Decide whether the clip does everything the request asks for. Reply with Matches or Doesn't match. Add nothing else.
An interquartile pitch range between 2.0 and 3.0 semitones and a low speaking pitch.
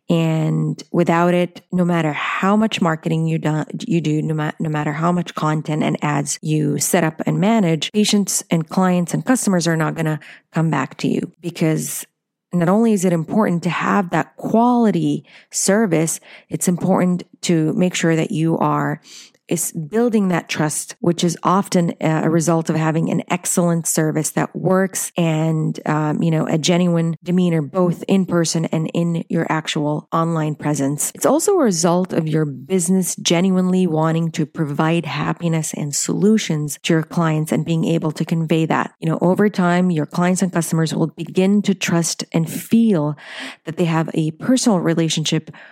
Doesn't match